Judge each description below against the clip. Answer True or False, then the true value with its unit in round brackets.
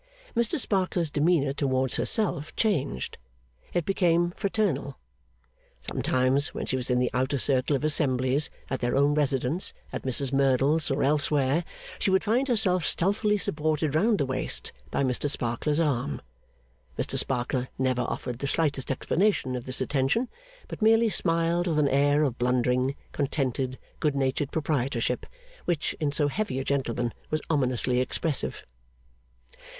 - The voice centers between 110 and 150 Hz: True (140 Hz)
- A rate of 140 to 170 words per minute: True (145 wpm)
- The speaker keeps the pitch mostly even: False (4.2 semitones)